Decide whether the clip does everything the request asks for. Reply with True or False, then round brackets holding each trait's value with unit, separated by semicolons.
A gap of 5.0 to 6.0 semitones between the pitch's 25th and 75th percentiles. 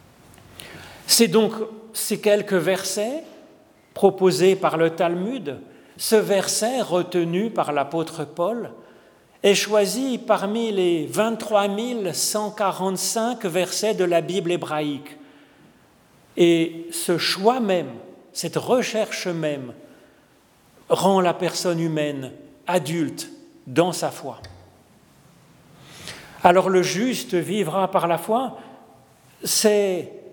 False (4.3 semitones)